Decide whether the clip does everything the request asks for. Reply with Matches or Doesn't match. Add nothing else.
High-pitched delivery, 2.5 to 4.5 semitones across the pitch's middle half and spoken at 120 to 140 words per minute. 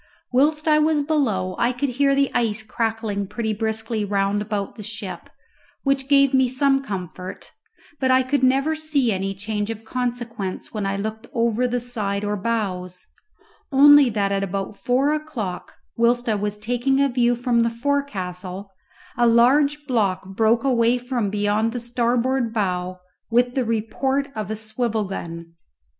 Doesn't match